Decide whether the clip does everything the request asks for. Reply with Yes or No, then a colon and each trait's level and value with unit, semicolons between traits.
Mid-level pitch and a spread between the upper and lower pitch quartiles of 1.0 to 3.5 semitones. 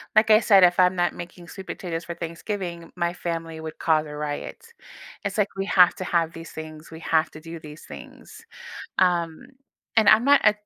Yes: medium, 170 Hz; average, 2.8 semitones